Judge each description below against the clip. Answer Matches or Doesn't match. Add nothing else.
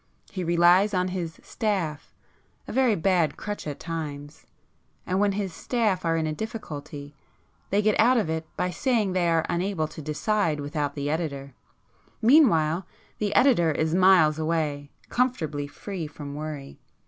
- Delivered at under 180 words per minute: Matches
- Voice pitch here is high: Doesn't match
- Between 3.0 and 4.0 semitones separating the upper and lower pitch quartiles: Doesn't match